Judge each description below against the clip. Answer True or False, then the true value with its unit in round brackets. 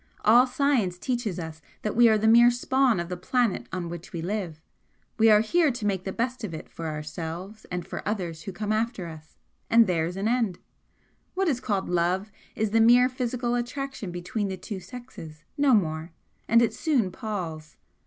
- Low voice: False (210 Hz)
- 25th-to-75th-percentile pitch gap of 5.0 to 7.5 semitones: True (5.4 semitones)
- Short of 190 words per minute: False (195 wpm)